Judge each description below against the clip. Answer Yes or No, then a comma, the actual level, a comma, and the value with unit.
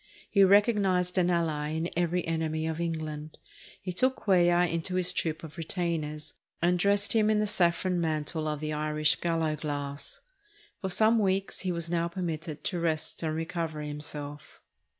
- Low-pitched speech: No, medium, 170 Hz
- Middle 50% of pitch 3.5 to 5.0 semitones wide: No, average, 2.8 semitones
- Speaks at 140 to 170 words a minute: Yes, average, 165 wpm